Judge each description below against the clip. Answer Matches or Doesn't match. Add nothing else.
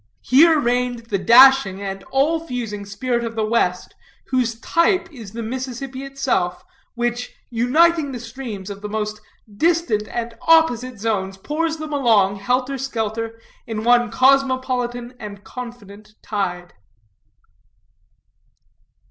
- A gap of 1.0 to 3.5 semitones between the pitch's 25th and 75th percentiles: Doesn't match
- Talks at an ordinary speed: Doesn't match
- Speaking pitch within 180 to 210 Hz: Doesn't match